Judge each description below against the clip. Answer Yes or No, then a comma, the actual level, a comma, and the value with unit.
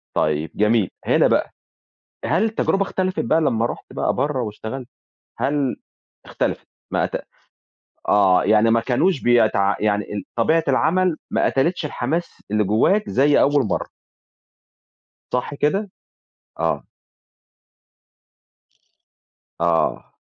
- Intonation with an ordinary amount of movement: No, wide, 6.8 semitones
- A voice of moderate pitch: No, low, 125 Hz